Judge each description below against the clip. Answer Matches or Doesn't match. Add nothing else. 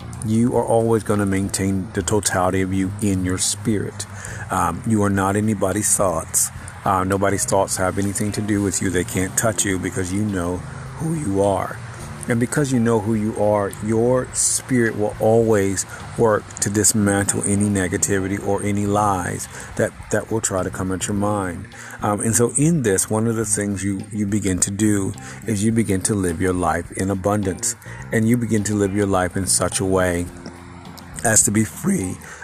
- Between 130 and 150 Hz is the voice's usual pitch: Doesn't match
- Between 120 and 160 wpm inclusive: Doesn't match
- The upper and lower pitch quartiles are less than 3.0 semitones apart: Matches